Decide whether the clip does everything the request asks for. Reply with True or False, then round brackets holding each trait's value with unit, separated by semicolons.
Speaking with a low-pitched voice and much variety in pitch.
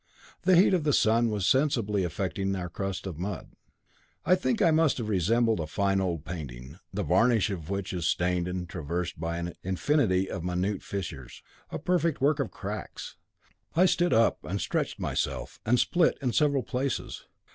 True (100 Hz; 6.6 semitones)